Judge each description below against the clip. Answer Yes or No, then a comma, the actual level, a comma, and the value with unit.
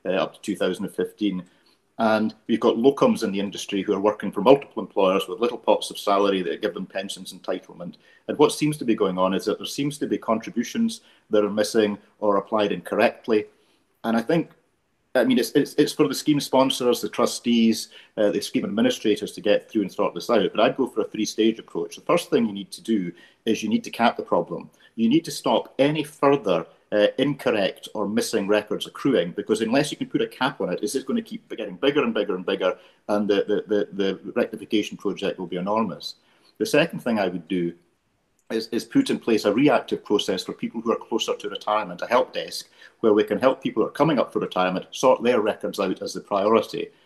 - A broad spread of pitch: Yes, wide, 6.6 semitones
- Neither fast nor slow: No, fast, 225 wpm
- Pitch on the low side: Yes, low, 115 Hz